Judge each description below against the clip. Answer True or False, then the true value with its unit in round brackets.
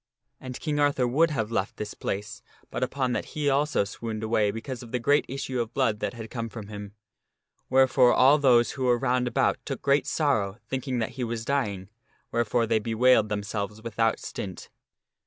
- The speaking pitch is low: True (120 Hz)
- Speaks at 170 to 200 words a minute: True (195 wpm)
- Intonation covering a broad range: False (3.4 semitones)